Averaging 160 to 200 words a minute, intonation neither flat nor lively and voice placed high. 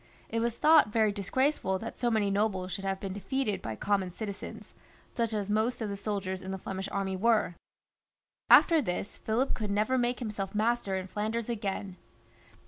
Yes: average, 180 wpm; average, 3.1 semitones; high, 210 Hz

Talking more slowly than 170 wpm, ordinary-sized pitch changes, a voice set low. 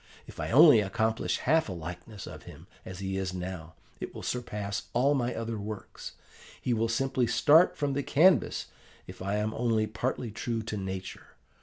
No: average, 180 wpm; average, 4.2 semitones; low, 110 Hz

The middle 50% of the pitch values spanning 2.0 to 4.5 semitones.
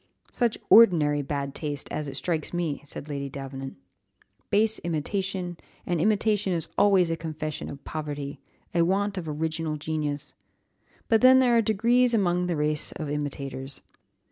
No: average, 5.2 semitones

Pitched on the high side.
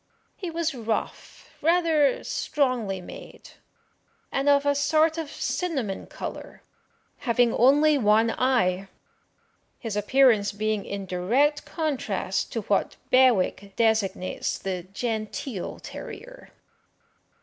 Yes: high, 245 Hz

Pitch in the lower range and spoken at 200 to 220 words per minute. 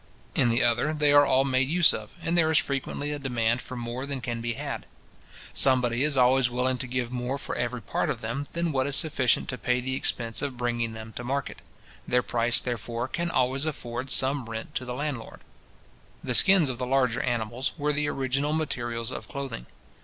Yes: low, 130 Hz; fast, 205 wpm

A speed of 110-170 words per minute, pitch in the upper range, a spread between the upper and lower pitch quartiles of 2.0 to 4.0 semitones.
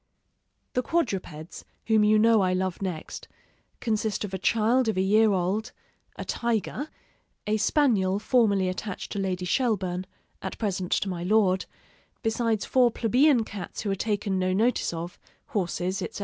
Yes: average, 155 wpm; high, 205 Hz; average, 3.3 semitones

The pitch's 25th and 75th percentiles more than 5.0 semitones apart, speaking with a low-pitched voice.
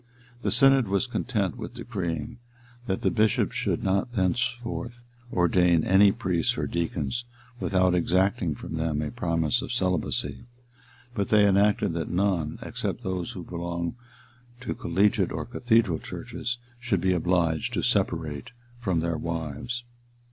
Yes: wide, 5.4 semitones; very low, 95 Hz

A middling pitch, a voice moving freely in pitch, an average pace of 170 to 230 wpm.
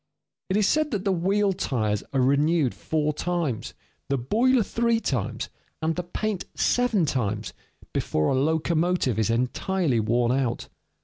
No: medium, 160 Hz; wide, 7.5 semitones; average, 145 wpm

